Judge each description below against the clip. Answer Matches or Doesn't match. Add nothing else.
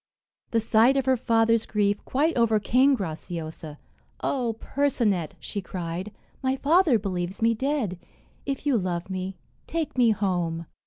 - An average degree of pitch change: Doesn't match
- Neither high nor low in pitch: Doesn't match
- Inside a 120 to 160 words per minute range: Matches